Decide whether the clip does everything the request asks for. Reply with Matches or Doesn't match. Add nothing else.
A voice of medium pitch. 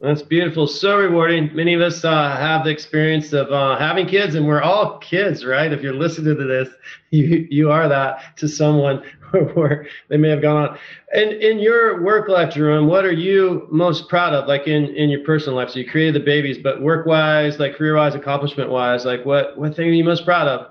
Matches